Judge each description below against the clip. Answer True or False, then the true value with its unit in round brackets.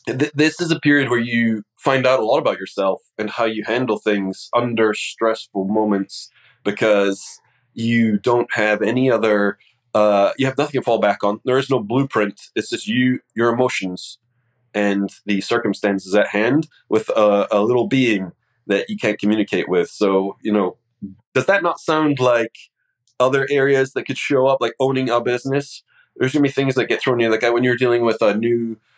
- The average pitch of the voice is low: True (115 Hz)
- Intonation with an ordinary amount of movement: True (3.6 semitones)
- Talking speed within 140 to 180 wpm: False (190 wpm)